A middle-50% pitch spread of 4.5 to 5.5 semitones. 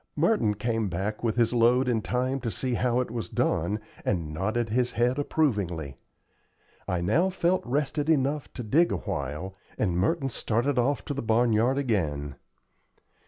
Yes: average, 4.8 semitones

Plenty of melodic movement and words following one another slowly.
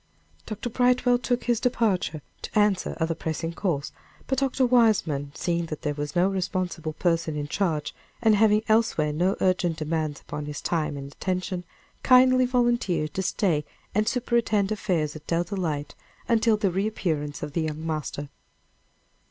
No: wide, 6.0 semitones; average, 155 wpm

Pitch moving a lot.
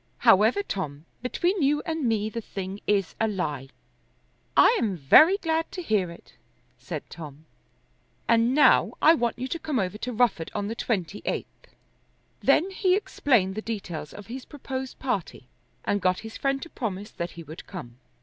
Yes: wide, 6.8 semitones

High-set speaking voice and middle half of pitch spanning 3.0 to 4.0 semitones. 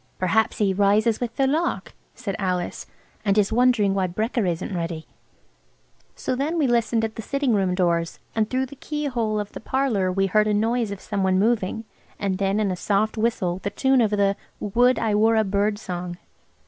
Yes: high, 210 Hz; average, 3.4 semitones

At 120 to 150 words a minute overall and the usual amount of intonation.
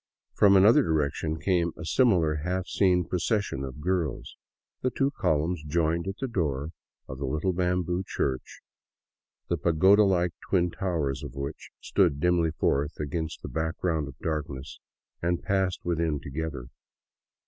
Yes: average, 145 wpm; average, 3.5 semitones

